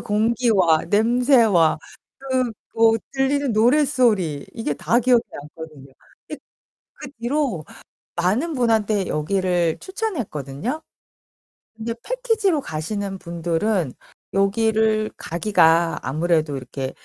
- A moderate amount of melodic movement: No, wide, 7.0 semitones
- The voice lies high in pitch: Yes, high, 215 Hz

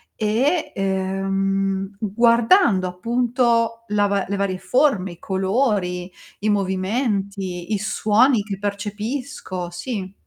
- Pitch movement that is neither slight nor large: Yes, average, 3.3 semitones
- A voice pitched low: No, high, 200 Hz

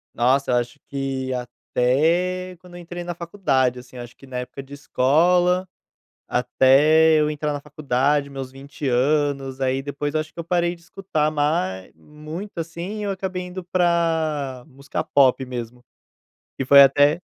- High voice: No, medium, 145 Hz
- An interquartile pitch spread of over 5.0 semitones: No, average, 4.5 semitones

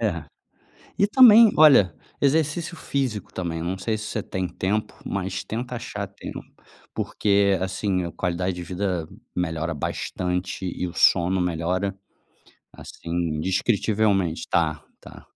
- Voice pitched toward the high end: No, very low, 95 Hz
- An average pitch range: Yes, average, 3.6 semitones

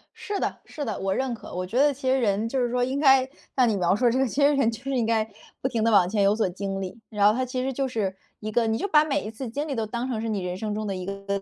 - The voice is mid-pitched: No, high, 230 Hz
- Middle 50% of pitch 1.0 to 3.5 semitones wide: No, average, 4.4 semitones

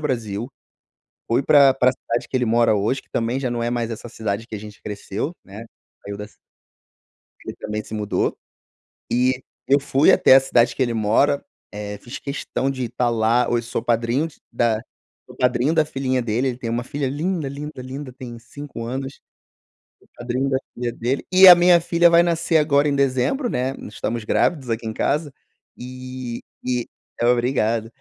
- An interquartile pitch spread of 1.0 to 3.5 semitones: Yes, average, 3.1 semitones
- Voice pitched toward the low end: Yes, low, 125 Hz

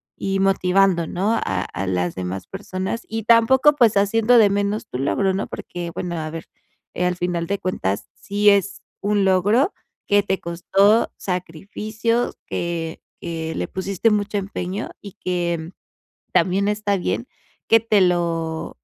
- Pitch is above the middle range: Yes, high, 195 Hz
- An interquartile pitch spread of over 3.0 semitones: Yes, average, 3.4 semitones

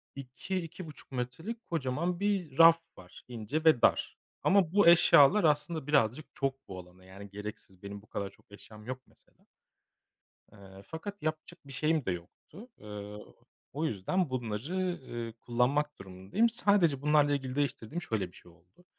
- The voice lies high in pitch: No, low, 135 Hz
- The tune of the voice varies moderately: No, wide, 7.8 semitones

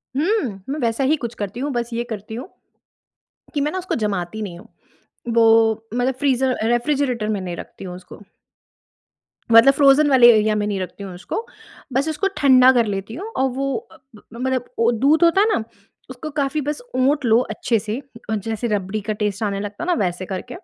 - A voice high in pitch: Yes, high, 240 Hz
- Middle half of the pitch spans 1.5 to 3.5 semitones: No, average, 4.6 semitones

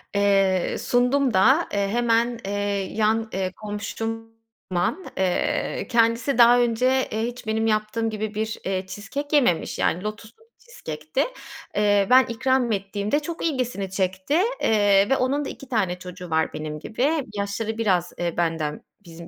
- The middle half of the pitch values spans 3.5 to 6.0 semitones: Yes, average, 4.1 semitones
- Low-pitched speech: No, high, 215 Hz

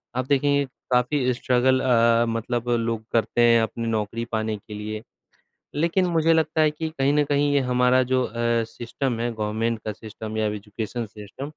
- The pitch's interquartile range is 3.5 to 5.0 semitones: Yes, average, 4.1 semitones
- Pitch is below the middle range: Yes, low, 120 Hz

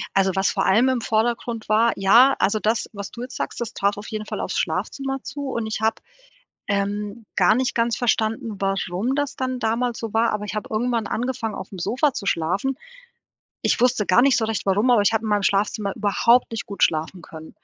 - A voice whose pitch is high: Yes, high, 220 Hz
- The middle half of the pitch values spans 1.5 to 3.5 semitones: Yes, average, 3.2 semitones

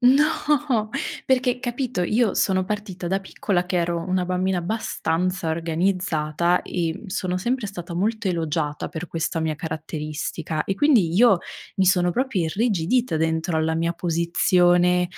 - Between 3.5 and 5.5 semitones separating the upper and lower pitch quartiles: Yes, average, 4.1 semitones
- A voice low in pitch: No, medium, 180 Hz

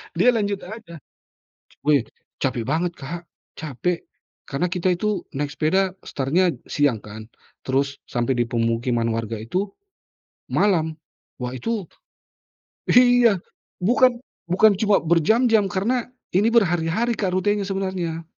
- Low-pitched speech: No, medium, 175 Hz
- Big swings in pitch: Yes, wide, 6.7 semitones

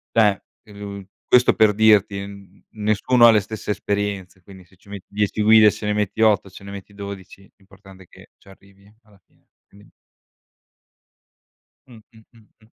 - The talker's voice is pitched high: No, low, 100 Hz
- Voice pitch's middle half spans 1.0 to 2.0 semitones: Yes, narrow, 1.5 semitones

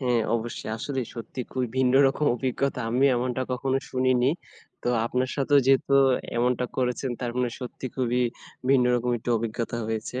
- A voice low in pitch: Yes, low, 125 Hz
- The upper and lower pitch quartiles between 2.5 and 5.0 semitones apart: No, narrow, 1.5 semitones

